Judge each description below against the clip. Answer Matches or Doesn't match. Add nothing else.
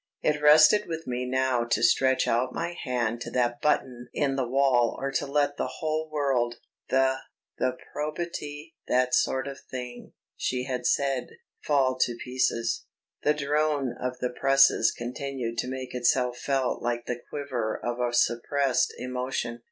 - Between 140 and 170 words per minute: Matches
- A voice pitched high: Doesn't match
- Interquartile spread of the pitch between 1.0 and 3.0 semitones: Matches